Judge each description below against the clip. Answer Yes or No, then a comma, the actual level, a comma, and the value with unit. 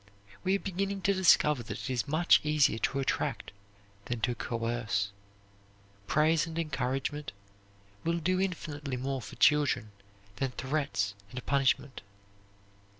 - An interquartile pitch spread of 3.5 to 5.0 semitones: Yes, average, 4.7 semitones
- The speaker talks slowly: Yes, slow, 130 wpm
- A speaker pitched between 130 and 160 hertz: Yes, medium, 140 Hz